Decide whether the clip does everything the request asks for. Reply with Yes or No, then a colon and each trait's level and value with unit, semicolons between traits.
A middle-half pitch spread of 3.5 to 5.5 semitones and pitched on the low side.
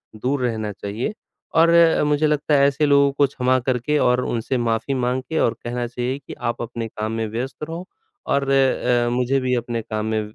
No: average, 3.0 semitones; low, 125 Hz